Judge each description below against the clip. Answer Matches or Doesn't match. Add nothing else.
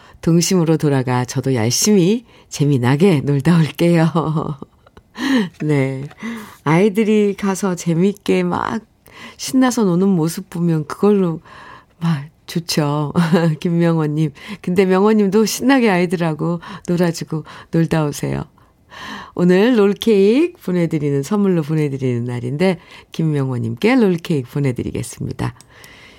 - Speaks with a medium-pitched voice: Matches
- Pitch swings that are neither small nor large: Matches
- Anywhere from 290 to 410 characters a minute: Doesn't match